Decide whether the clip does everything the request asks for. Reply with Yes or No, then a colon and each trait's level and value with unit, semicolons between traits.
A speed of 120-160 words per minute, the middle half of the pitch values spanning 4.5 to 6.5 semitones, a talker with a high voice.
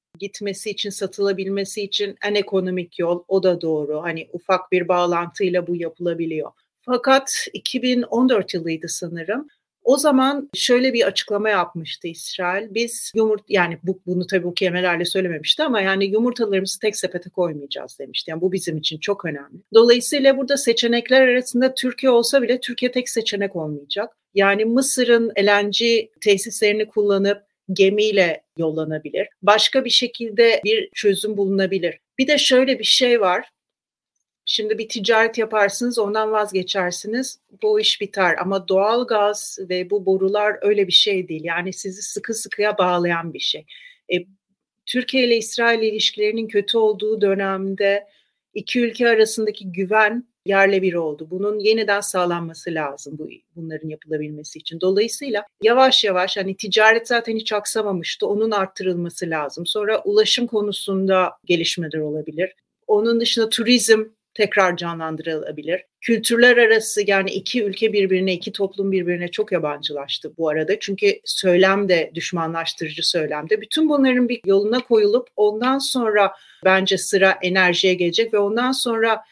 No: average, 135 wpm; average, 3.9 semitones; high, 200 Hz